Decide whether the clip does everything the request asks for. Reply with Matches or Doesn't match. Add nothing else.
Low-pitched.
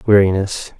Matches